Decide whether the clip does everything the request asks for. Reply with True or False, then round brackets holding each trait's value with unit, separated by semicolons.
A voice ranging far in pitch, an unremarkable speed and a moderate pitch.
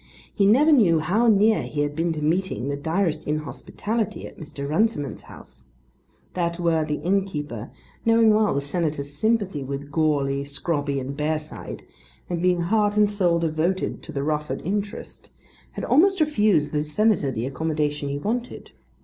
True (5.9 semitones; 155 wpm; 165 Hz)